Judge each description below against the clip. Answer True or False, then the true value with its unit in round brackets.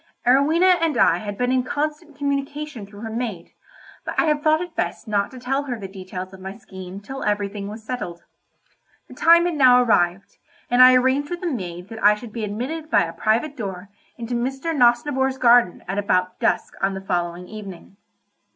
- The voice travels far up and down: True (5.9 semitones)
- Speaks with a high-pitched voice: True (235 Hz)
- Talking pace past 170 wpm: True (195 wpm)